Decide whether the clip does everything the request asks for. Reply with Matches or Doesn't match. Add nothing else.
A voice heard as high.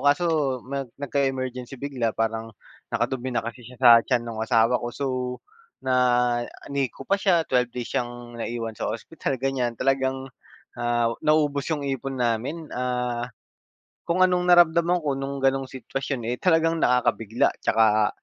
Doesn't match